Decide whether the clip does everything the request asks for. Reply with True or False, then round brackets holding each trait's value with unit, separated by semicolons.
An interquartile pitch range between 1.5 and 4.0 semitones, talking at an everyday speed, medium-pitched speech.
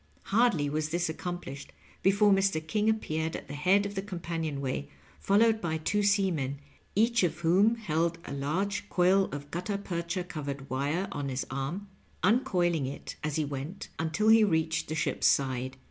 False (5.3 semitones; 170 wpm; 170 Hz)